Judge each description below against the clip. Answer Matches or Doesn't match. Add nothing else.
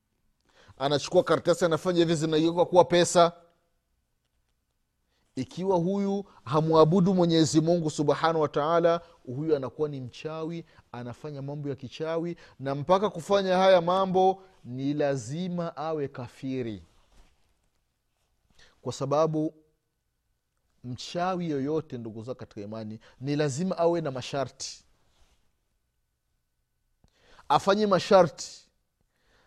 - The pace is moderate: Doesn't match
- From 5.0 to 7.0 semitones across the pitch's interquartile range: Matches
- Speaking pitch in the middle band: Matches